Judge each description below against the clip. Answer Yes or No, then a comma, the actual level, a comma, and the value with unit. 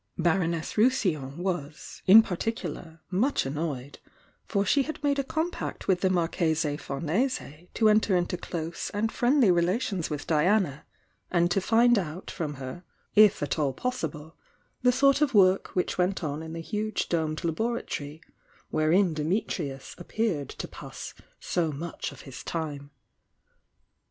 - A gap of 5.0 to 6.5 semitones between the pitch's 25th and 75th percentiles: Yes, wide, 5.6 semitones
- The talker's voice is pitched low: No, medium, 175 Hz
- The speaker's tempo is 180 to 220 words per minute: No, average, 150 wpm